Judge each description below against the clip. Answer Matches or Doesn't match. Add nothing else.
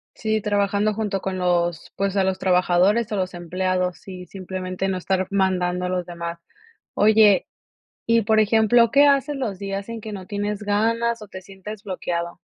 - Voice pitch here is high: Matches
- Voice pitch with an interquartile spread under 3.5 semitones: Matches